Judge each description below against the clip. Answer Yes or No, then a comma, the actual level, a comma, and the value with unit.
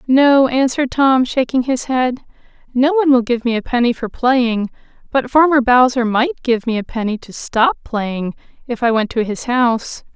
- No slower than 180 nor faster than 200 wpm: Yes, average, 190 wpm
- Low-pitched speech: No, very high, 250 Hz